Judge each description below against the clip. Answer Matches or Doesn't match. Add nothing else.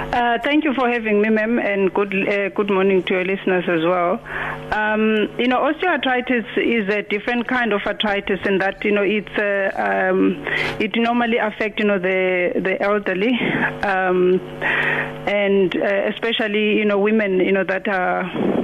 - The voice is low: Doesn't match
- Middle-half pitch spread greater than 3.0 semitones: Doesn't match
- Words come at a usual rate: Matches